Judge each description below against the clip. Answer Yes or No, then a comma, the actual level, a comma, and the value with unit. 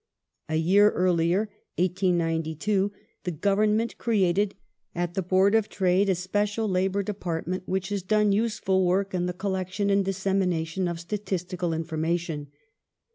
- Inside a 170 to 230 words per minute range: No, average, 140 wpm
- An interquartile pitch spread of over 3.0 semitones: No, narrow, 2.5 semitones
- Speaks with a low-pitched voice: No, medium, 185 Hz